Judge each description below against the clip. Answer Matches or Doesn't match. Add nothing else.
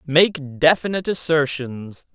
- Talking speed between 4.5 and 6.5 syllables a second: Doesn't match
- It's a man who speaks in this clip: Matches